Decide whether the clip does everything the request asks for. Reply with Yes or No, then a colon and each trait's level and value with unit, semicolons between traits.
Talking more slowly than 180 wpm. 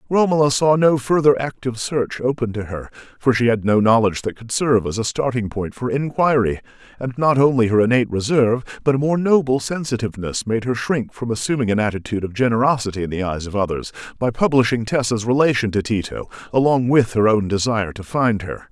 No: average, 200 wpm